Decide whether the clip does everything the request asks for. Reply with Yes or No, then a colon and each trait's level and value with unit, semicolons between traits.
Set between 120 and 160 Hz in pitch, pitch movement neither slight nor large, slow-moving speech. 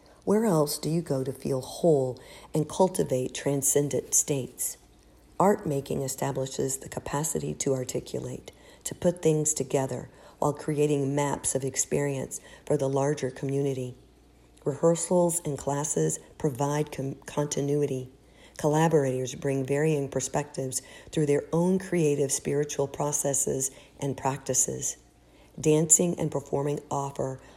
No: medium, 140 Hz; narrow, 2.2 semitones; slow, 120 wpm